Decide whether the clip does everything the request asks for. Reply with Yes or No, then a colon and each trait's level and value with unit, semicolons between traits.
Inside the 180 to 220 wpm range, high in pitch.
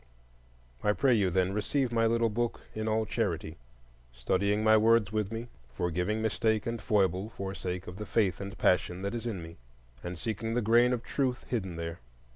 No: average, 190 wpm; low, 105 Hz